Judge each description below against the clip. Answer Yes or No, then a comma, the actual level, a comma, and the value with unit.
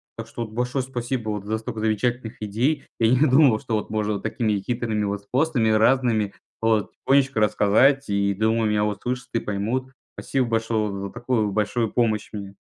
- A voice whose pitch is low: Yes, low, 110 Hz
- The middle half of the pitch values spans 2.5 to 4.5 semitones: Yes, average, 2.8 semitones